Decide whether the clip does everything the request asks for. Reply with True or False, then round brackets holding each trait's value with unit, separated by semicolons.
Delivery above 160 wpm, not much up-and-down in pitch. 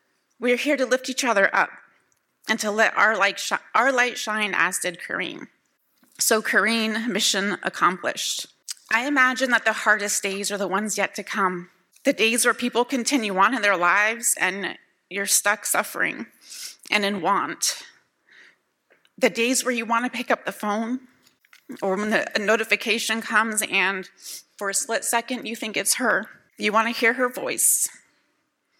False (175 wpm; 3.5 semitones)